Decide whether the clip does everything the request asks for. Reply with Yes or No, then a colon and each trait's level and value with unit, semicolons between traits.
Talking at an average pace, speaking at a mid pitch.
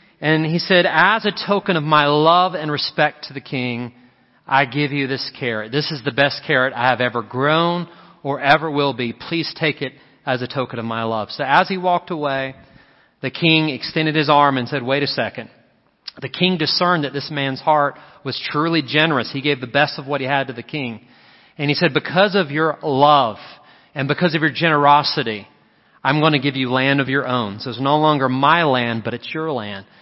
No: fast, 215 wpm; medium, 145 Hz